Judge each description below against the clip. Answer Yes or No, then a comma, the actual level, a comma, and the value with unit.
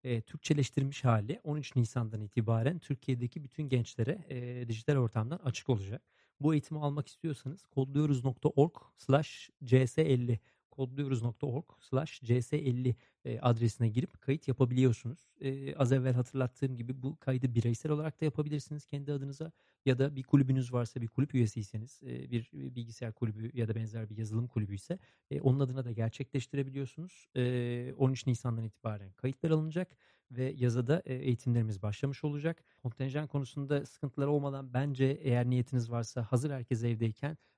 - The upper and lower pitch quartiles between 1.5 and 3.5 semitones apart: Yes, average, 3.1 semitones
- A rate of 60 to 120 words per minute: No, average, 130 wpm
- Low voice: Yes, low, 130 Hz